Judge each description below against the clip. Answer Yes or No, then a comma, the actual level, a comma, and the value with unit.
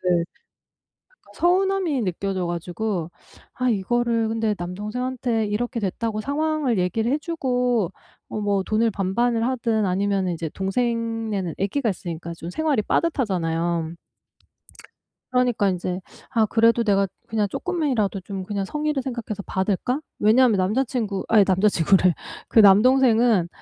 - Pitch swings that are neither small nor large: Yes, average, 4.4 semitones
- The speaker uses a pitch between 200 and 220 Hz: Yes, high, 215 Hz